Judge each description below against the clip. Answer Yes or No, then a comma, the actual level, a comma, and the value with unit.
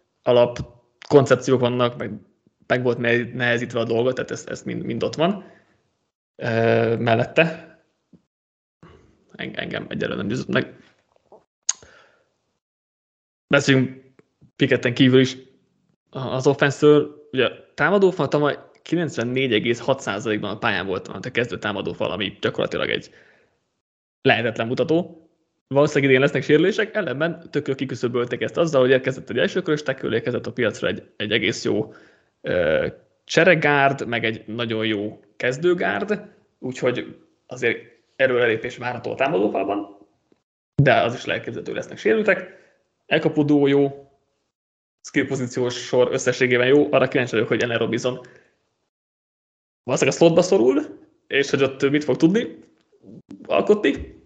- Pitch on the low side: Yes, low, 130 Hz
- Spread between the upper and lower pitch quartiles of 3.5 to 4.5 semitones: Yes, average, 4.2 semitones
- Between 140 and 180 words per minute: No, average, 115 wpm